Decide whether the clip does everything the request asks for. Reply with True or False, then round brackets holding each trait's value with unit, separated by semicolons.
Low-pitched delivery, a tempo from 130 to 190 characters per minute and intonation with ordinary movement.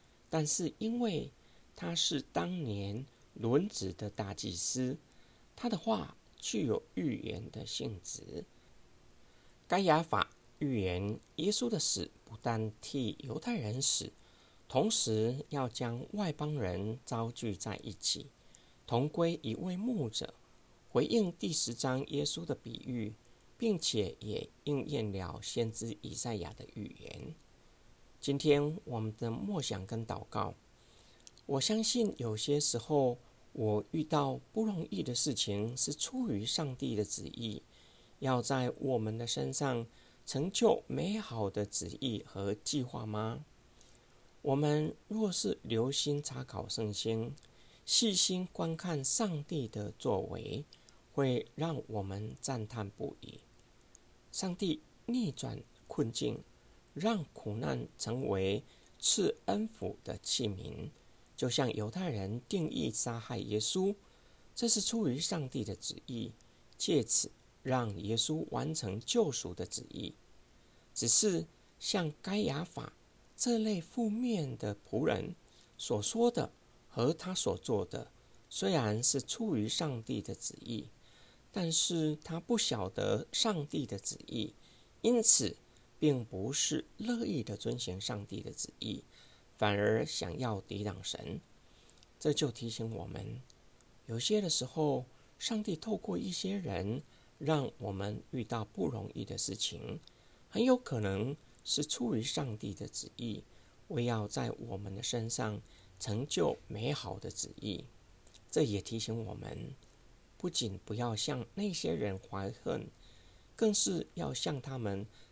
False (125 Hz; 185 characters per minute; 6.8 semitones)